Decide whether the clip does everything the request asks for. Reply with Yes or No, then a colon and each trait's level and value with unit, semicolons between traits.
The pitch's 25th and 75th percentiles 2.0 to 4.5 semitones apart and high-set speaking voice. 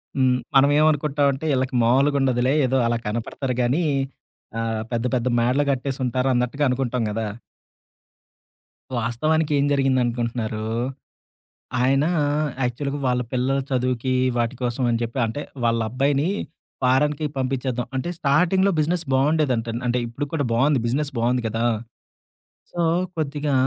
No: average, 2.9 semitones; low, 130 Hz